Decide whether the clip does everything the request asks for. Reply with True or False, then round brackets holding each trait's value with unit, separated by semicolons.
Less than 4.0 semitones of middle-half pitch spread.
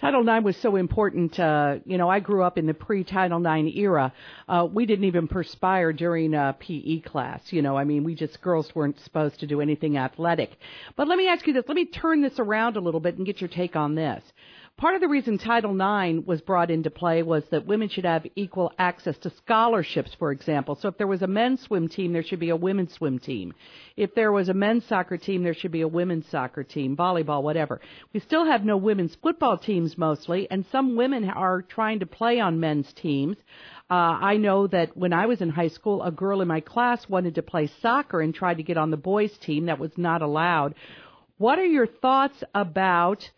False (4.4 semitones)